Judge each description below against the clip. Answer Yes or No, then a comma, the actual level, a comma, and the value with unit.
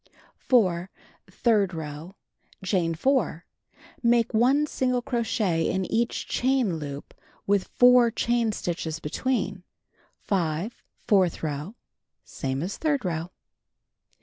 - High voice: Yes, high, 200 Hz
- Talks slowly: Yes, slow, 105 wpm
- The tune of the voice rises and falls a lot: Yes, wide, 6.5 semitones